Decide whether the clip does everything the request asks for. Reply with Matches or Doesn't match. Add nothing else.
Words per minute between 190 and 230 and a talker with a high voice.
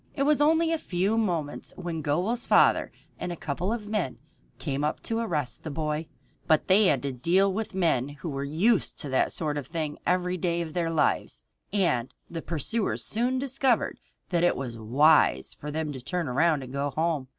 Doesn't match